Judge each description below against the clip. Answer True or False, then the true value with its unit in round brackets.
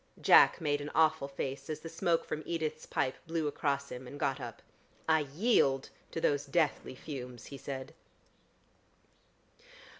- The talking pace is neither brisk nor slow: True (150 wpm)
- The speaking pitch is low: False (145 Hz)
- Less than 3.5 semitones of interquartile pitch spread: True (2.8 semitones)